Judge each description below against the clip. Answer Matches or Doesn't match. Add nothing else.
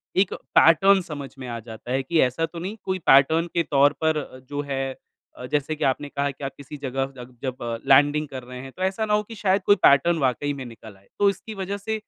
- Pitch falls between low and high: Matches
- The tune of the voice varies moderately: Doesn't match